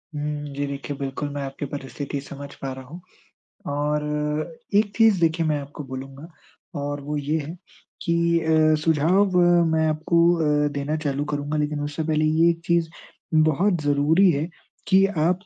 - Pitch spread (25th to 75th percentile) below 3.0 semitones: Yes, narrow, 2.4 semitones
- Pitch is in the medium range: Yes, medium, 150 Hz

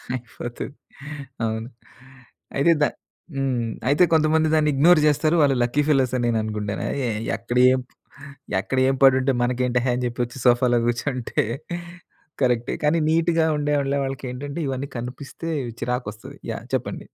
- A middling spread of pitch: Yes, average, 3.1 semitones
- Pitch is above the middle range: No, low, 130 Hz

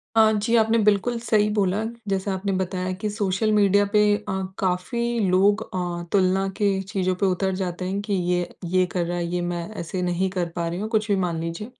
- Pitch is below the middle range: No, high, 190 Hz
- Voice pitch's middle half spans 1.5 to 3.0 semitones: Yes, average, 2.7 semitones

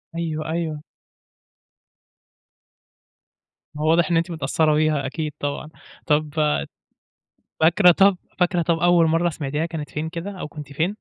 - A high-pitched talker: No, medium, 160 Hz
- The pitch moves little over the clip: Yes, narrow, 2.1 semitones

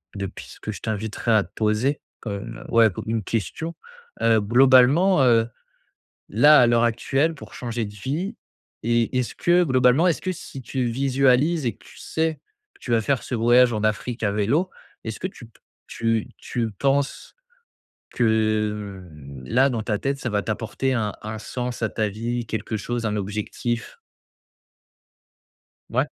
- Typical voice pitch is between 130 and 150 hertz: No, low, 115 Hz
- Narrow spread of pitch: No, average, 3.7 semitones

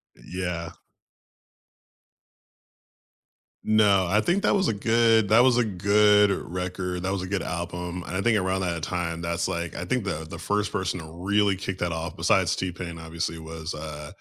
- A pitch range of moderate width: Yes, average, 3.3 semitones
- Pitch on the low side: Yes, very low, 90 Hz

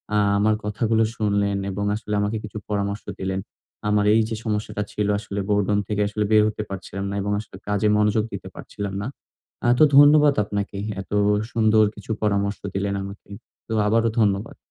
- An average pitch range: No, narrow, 1.3 semitones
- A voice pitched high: No, low, 105 Hz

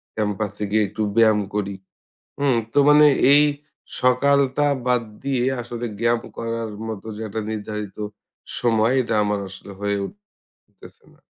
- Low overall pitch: Yes, low, 115 Hz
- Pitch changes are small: No, average, 3.2 semitones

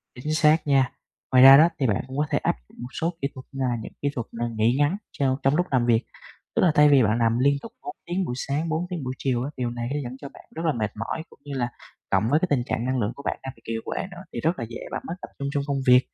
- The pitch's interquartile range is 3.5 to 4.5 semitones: Yes, average, 3.9 semitones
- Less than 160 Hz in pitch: Yes, low, 135 Hz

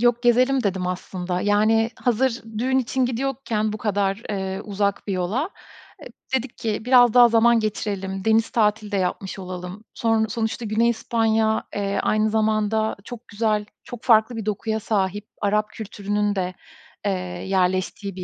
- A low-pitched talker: No, high, 215 Hz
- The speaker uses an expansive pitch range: No, narrow, 2.5 semitones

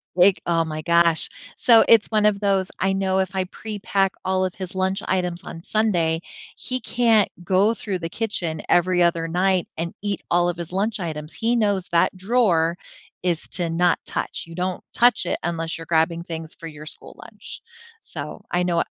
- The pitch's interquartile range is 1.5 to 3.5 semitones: Yes, average, 2.9 semitones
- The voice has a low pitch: No, medium, 180 Hz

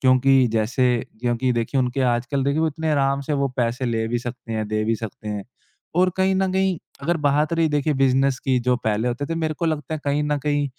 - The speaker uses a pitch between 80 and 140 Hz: Yes, low, 135 Hz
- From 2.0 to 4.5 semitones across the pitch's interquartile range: Yes, average, 3.9 semitones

